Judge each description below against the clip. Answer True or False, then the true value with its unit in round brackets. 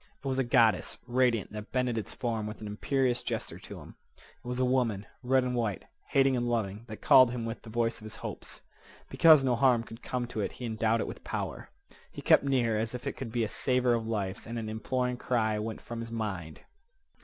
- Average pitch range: False (2.3 semitones)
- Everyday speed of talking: False (230 wpm)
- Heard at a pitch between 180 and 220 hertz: False (115 Hz)